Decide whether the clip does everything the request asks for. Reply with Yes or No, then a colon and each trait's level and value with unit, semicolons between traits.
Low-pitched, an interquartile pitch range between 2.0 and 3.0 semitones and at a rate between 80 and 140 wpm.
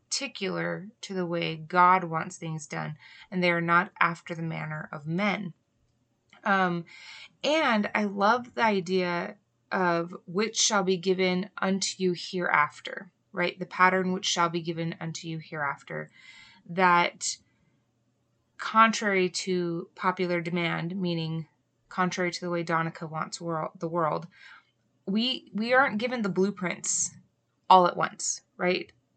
No: medium, 180 Hz; narrow, 2.5 semitones; slow, 135 wpm